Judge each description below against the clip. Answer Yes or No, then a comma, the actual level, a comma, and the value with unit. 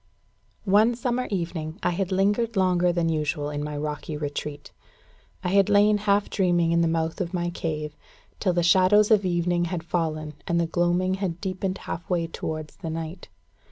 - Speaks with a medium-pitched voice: Yes, medium, 175 Hz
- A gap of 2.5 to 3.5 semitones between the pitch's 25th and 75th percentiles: Yes, average, 3.0 semitones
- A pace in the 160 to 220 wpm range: Yes, average, 180 wpm